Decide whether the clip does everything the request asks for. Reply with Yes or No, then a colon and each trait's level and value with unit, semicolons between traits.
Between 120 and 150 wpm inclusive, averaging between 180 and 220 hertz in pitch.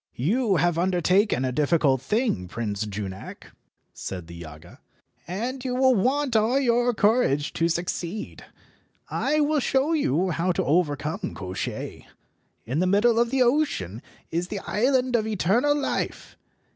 Yes: average, 145 wpm; medium, 185 Hz